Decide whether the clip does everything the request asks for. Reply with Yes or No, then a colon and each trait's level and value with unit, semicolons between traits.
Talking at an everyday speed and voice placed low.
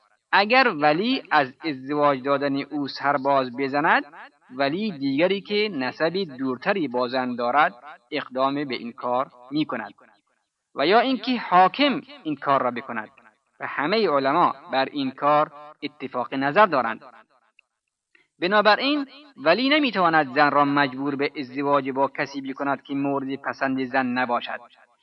No: average, 130 wpm; medium, 145 Hz